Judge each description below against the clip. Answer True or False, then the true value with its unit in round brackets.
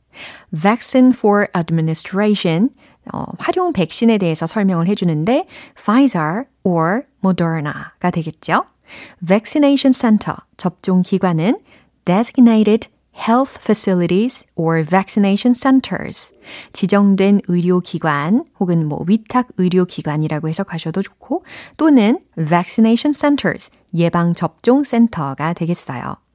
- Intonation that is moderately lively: False (6.3 semitones)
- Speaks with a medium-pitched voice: False (200 Hz)